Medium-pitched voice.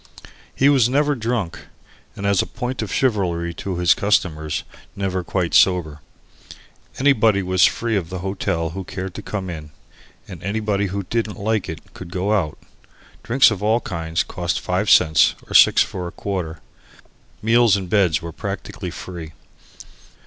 No: very low, 95 Hz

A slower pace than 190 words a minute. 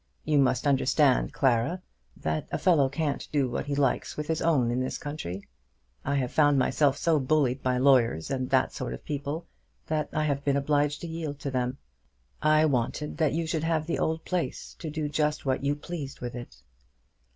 No: average, 195 wpm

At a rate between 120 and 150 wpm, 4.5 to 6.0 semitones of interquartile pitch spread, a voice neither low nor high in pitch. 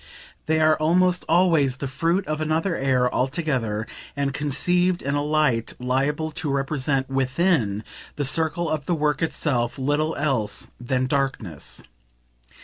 No: average, 140 wpm; average, 3.2 semitones; medium, 145 Hz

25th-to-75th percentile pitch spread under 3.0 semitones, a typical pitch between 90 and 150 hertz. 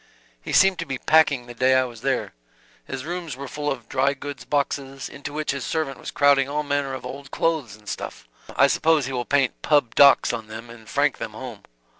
Yes: narrow, 2.6 semitones; low, 135 Hz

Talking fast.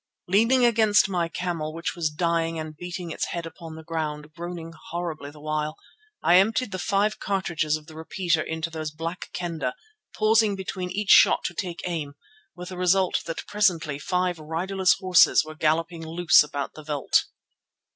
No: average, 170 wpm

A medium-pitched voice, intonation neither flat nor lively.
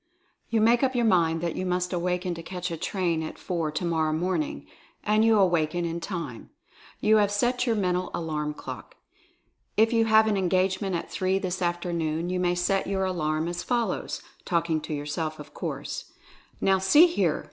Yes: medium, 180 Hz; average, 3.1 semitones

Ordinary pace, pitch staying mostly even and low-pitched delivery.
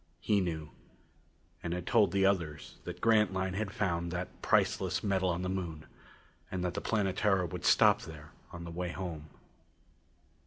Yes: average, 160 wpm; narrow, 2.3 semitones; very low, 90 Hz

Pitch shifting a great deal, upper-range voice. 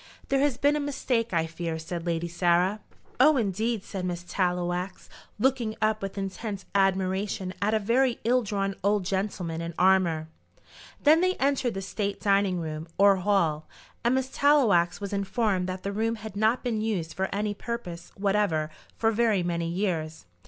No: average, 4.1 semitones; high, 195 Hz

